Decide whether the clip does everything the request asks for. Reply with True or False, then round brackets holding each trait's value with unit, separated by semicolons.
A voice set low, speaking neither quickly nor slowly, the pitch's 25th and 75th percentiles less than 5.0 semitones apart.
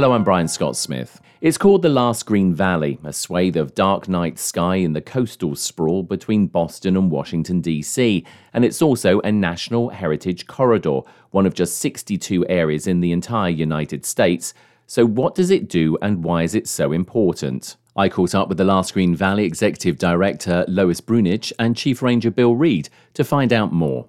False (95 Hz; 185 wpm; 5.4 semitones)